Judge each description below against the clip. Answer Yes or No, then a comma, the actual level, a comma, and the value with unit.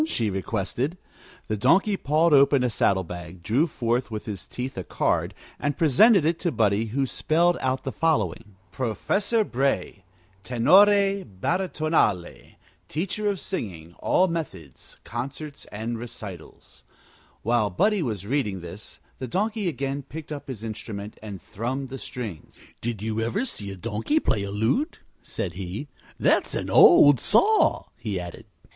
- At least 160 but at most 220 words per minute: No, average, 150 wpm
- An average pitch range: No, wide, 7.7 semitones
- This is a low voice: Yes, low, 125 Hz